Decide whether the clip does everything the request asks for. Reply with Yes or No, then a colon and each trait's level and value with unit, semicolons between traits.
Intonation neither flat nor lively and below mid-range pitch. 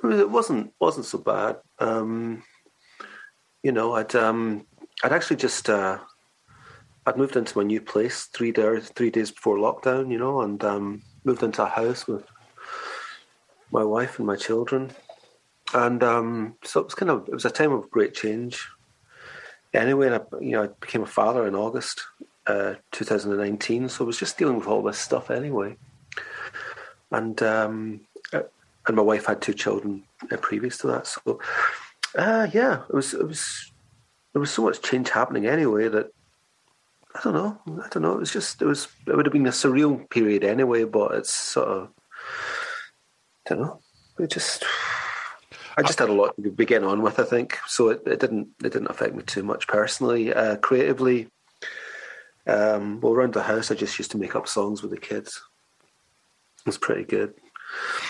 Yes: average, 3.5 semitones; low, 115 Hz